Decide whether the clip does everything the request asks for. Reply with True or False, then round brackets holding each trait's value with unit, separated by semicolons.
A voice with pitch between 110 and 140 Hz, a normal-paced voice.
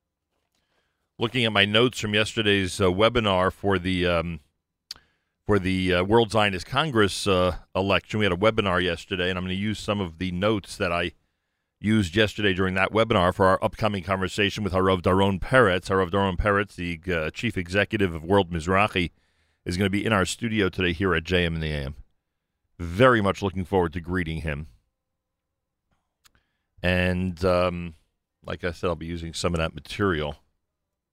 False (90 Hz; 175 wpm)